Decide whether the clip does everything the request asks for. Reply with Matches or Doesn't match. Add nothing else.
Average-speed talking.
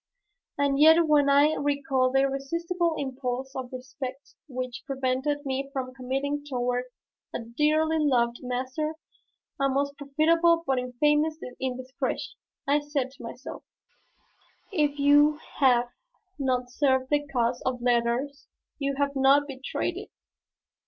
Doesn't match